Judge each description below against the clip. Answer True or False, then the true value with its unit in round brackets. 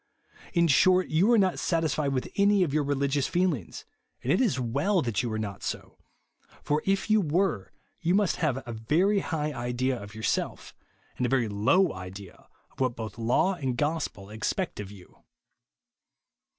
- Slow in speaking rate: False (175 wpm)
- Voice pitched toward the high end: False (145 Hz)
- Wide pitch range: True (7.4 semitones)